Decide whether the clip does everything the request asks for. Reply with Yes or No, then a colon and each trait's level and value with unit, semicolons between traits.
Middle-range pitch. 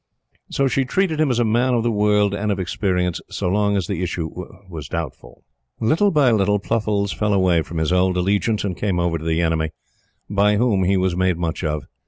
No: low, 100 Hz